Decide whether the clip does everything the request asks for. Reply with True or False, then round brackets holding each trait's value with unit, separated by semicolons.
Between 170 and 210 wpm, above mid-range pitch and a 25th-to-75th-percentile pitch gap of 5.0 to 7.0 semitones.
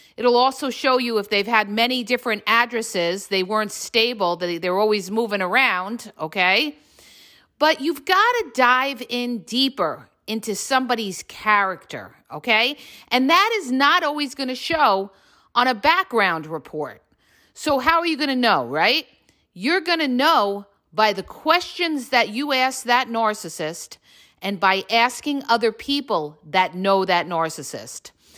False (150 wpm; 230 Hz; 5.5 semitones)